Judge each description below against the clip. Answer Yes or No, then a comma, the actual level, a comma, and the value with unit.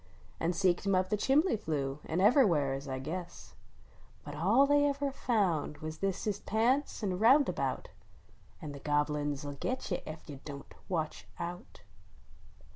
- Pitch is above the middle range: No, medium, 180 Hz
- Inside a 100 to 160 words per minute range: No, average, 175 wpm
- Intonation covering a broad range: Yes, wide, 7.0 semitones